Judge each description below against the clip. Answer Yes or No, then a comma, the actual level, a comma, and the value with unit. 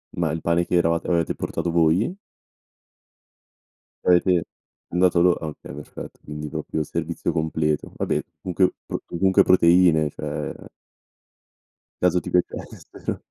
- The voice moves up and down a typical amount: No, narrow, 2.1 semitones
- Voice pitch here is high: No, very low, 85 Hz